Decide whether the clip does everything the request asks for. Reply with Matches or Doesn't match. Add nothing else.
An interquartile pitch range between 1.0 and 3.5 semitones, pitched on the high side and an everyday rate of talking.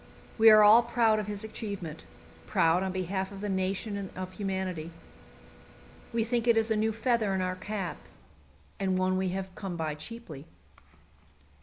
Matches